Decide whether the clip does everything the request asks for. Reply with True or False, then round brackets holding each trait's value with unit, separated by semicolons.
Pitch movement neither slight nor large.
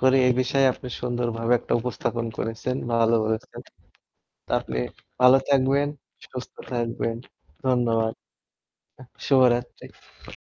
False (1.9 semitones)